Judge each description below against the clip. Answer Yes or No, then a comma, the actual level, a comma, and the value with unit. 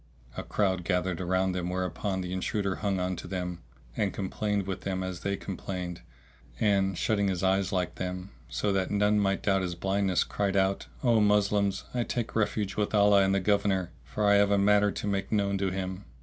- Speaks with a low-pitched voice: Yes, very low, 95 Hz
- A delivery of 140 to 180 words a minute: No, average, 200 wpm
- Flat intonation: Yes, narrow, 1.7 semitones